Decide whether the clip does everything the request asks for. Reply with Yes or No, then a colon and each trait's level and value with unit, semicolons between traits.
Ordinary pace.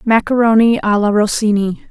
No: slow, 125 wpm